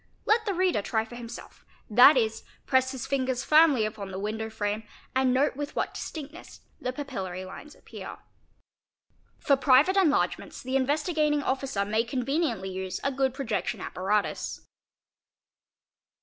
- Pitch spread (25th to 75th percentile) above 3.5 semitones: Yes, average, 4.8 semitones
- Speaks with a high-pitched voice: Yes, very high, 260 Hz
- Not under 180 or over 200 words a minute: No, average, 140 wpm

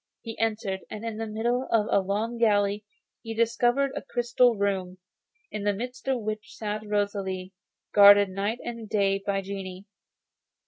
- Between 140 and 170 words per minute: Yes, average, 155 wpm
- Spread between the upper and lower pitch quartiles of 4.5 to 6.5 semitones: No, narrow, 2.4 semitones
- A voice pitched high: Yes, high, 210 Hz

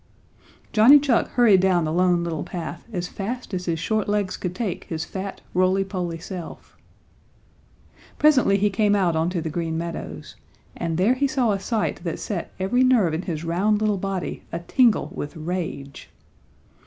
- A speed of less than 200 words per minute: Yes, average, 170 wpm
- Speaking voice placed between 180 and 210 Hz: Yes, medium, 185 Hz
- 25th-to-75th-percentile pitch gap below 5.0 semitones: Yes, average, 4.0 semitones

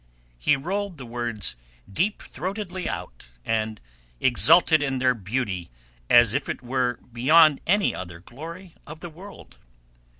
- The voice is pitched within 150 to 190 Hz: No, low, 135 Hz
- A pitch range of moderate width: No, wide, 6.8 semitones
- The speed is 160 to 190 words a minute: No, slow, 135 wpm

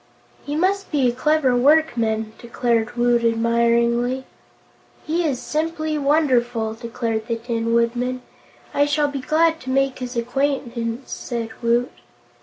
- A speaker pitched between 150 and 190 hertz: No, high, 245 Hz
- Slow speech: Yes, slow, 130 wpm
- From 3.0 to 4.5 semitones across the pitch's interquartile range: Yes, average, 3.7 semitones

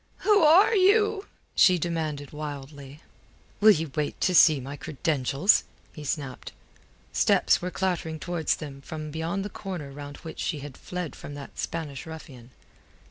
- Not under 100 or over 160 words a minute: Yes, average, 150 wpm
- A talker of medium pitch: Yes, medium, 155 Hz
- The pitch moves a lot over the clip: No, average, 4.0 semitones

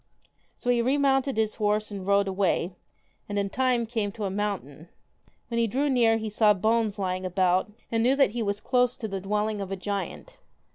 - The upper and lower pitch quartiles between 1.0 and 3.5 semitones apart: Yes, average, 3.2 semitones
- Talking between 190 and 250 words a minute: Yes, average, 200 wpm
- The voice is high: Yes, high, 210 Hz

